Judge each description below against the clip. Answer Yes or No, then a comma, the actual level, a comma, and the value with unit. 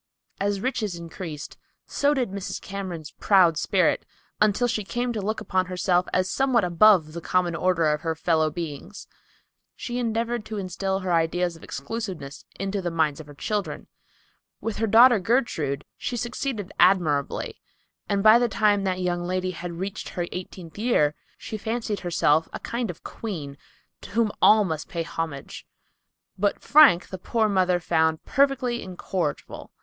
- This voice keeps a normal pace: Yes, average, 160 wpm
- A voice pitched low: No, medium, 185 Hz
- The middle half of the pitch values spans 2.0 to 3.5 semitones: No, average, 4.6 semitones